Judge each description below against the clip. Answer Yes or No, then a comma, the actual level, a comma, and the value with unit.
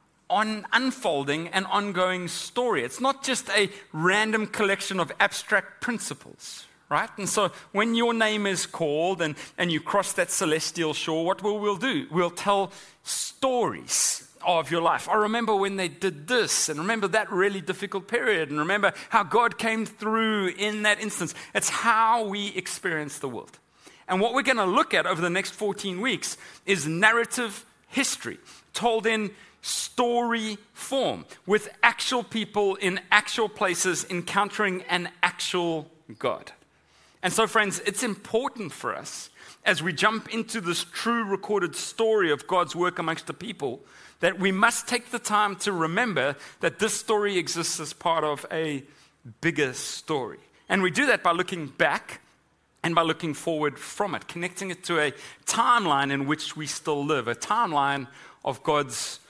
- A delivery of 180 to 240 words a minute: No, average, 165 wpm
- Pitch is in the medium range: No, high, 195 Hz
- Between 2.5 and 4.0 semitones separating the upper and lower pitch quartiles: No, average, 4.4 semitones